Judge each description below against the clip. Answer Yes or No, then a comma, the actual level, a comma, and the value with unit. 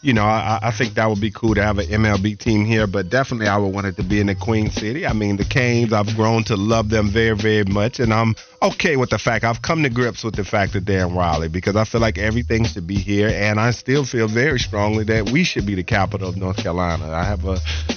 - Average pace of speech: No, fast, 275 wpm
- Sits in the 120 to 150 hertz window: No, low, 110 Hz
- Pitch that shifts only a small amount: Yes, narrow, 2.2 semitones